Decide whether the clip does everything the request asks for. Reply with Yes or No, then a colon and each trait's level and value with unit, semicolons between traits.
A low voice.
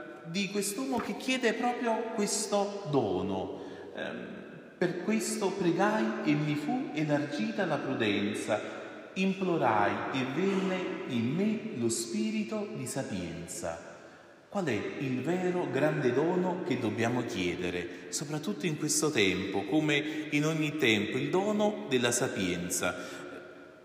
No: medium, 150 Hz